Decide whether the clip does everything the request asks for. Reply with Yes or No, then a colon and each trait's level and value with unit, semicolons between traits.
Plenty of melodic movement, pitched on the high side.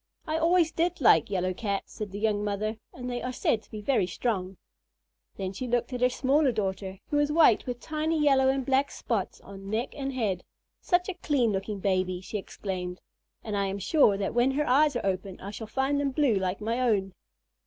Yes: wide, 5.7 semitones; high, 230 Hz